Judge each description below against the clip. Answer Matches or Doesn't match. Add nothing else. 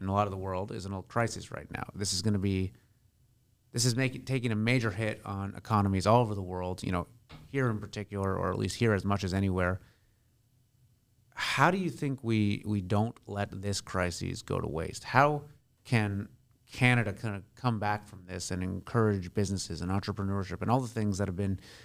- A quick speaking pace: Matches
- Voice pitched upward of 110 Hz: Doesn't match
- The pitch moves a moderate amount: Matches